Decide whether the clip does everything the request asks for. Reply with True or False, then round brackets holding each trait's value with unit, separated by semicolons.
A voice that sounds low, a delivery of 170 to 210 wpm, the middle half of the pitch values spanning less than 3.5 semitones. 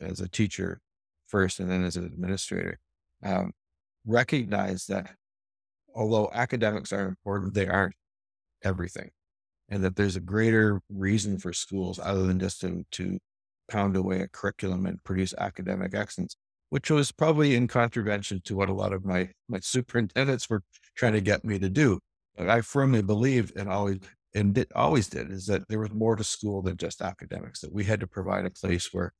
True (100 Hz; 180 wpm; 2.6 semitones)